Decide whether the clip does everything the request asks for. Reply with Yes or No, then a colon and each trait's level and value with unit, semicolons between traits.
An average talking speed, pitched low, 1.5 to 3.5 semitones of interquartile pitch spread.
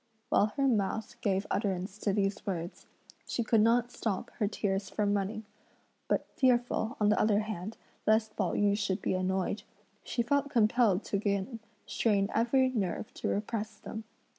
No: average, 165 wpm; high, 210 Hz; narrow, 2.5 semitones